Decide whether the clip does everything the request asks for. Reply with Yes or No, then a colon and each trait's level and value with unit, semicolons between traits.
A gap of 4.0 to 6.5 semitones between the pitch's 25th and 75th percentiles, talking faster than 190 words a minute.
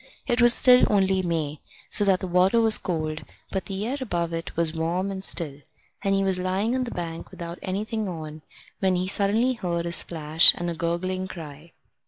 No: average, 3.0 semitones; average, 200 wpm